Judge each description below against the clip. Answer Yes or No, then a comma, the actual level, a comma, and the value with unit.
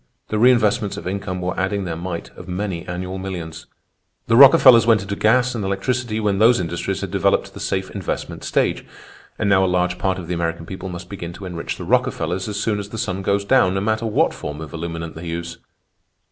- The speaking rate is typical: No, fast, 215 wpm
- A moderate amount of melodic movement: Yes, average, 3.3 semitones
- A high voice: No, very low, 95 Hz